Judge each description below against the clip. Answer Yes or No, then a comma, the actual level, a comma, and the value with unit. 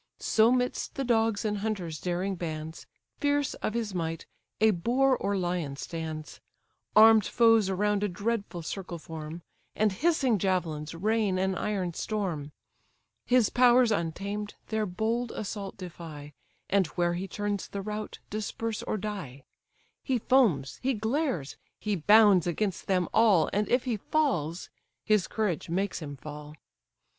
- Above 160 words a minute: No, average, 145 wpm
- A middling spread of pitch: Yes, average, 4.4 semitones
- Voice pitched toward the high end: Yes, high, 200 Hz